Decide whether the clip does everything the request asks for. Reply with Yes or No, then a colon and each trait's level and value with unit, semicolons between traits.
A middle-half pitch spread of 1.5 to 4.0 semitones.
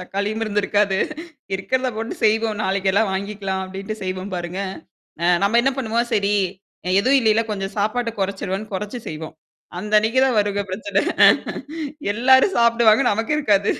Yes: average, 2.7 semitones